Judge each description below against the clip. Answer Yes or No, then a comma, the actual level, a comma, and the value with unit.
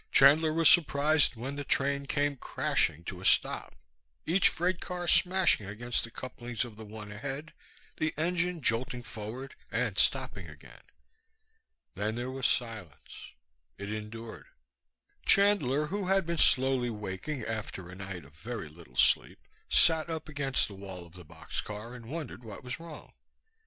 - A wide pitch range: Yes, wide, 6.6 semitones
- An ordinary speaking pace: Yes, average, 155 wpm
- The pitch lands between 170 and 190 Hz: No, low, 125 Hz